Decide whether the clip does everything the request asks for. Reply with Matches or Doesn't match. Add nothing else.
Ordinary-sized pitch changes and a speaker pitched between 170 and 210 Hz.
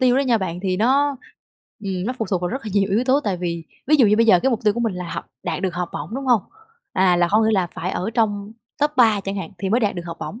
Matches